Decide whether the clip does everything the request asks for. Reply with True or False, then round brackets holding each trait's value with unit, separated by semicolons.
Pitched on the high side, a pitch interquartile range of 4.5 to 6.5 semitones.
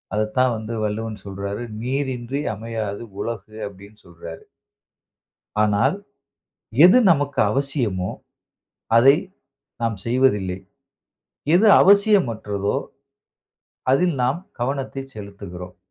False (115 Hz; 5.1 semitones)